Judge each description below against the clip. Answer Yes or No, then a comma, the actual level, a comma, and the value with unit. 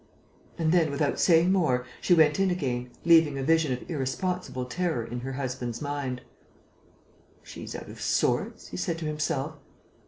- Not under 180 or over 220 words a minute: No, average, 160 wpm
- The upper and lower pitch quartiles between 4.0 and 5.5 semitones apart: Yes, average, 4.4 semitones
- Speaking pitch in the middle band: Yes, medium, 150 Hz